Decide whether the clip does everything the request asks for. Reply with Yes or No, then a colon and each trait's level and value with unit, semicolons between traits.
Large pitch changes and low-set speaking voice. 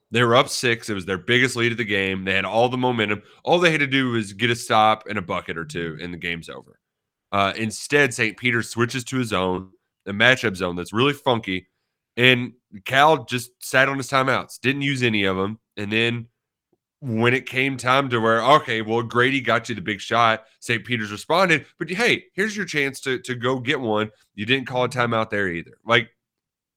No: average, 3.5 semitones; low, 120 Hz